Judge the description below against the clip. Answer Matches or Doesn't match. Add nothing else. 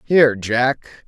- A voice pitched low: Matches